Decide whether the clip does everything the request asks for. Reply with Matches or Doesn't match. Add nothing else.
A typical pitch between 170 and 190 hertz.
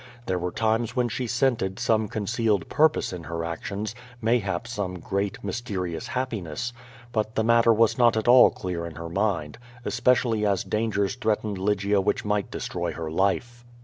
Doesn't match